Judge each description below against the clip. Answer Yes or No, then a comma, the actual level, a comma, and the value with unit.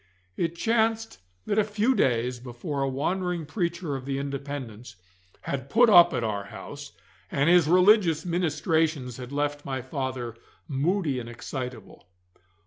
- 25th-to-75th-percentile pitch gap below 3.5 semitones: No, wide, 5.4 semitones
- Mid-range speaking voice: Yes, medium, 145 Hz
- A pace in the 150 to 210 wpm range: No, average, 140 wpm